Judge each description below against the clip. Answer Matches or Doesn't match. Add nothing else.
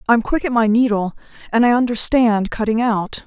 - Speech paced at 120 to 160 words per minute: Doesn't match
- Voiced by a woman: Matches